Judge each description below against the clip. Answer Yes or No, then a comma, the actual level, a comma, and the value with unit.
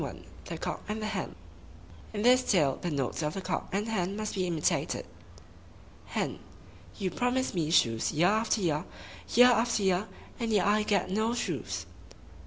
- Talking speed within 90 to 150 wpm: No, average, 165 wpm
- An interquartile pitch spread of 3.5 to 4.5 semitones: Yes, average, 4.0 semitones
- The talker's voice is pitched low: No, high, 200 Hz